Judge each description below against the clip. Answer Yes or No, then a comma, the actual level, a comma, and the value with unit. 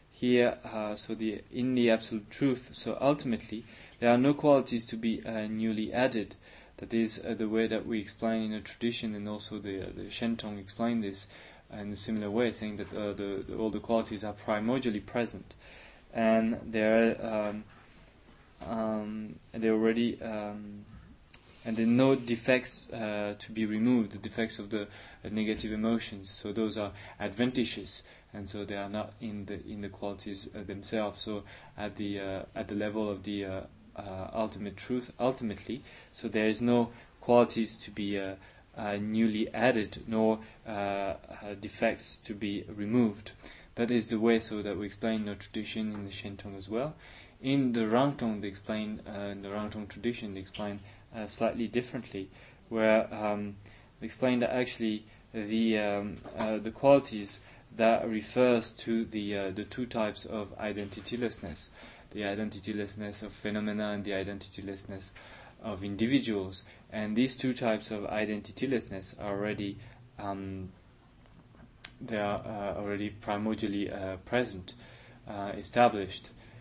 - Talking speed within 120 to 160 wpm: Yes, average, 155 wpm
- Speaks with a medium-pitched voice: No, low, 110 Hz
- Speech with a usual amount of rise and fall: No, narrow, 2.0 semitones